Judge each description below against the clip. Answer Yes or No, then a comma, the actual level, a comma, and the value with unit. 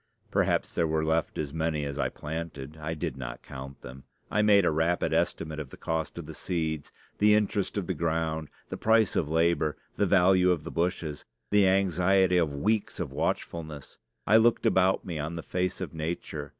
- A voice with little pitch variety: No, average, 3.3 semitones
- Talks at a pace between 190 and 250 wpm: Yes, average, 195 wpm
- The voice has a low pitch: Yes, very low, 80 Hz